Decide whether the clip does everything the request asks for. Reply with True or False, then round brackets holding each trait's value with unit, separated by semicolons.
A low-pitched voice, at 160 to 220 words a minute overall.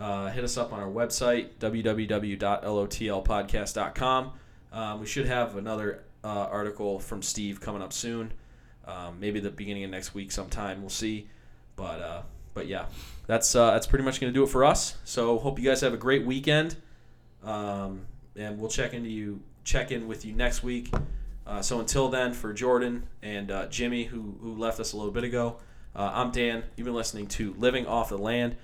True (110 Hz; 195 wpm)